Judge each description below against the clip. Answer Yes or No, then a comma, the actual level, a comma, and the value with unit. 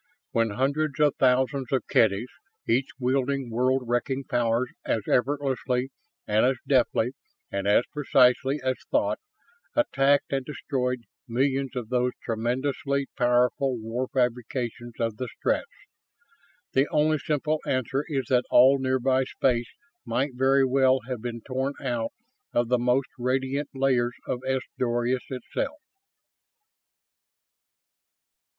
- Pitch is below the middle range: Yes, low, 130 Hz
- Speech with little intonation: Yes, narrow, 2.0 semitones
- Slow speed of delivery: Yes, slow, 125 wpm